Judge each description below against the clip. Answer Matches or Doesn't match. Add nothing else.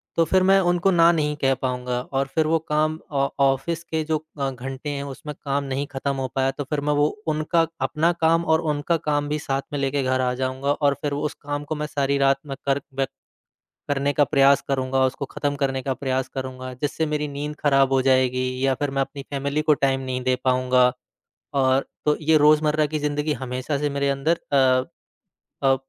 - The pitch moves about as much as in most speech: Doesn't match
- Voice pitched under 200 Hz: Matches